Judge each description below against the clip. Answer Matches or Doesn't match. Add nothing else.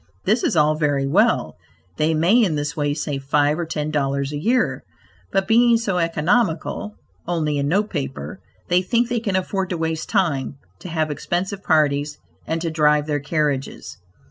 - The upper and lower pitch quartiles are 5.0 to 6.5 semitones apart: Doesn't match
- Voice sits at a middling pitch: Matches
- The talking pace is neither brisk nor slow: Matches